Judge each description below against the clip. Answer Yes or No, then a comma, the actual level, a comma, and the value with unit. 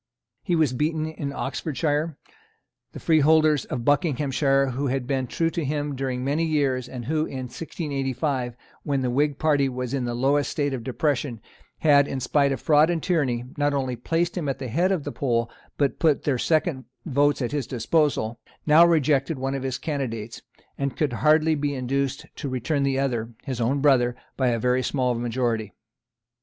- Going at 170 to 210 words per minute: Yes, average, 185 wpm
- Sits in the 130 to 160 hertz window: Yes, medium, 140 Hz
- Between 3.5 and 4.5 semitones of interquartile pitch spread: No, average, 2.9 semitones